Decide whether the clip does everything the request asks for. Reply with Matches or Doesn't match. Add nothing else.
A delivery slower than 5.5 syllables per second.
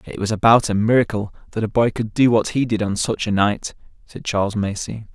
Doesn't match